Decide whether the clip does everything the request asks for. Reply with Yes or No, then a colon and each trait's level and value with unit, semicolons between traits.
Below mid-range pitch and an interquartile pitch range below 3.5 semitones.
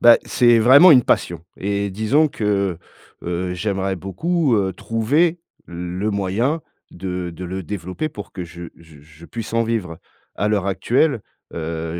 No: low, 100 Hz; average, 4.8 semitones